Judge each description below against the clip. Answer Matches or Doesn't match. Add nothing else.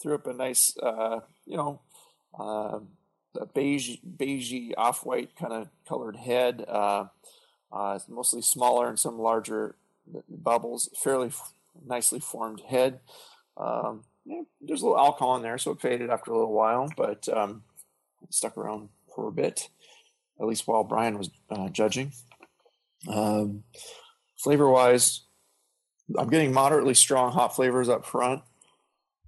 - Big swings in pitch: Doesn't match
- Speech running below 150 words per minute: Matches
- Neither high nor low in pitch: Doesn't match